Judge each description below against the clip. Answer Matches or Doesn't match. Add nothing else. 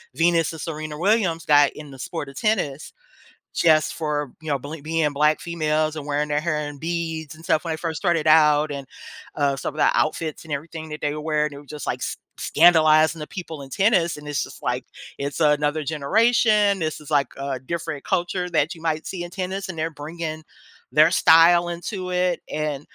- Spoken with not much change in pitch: Matches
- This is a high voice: Doesn't match